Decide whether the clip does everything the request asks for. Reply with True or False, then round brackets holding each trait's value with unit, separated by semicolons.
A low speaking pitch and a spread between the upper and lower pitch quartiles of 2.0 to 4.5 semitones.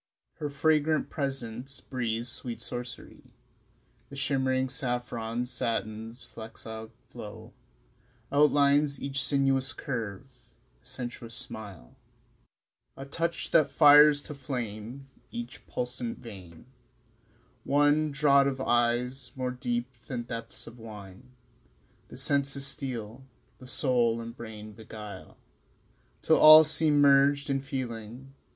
True (125 Hz; 3.1 semitones)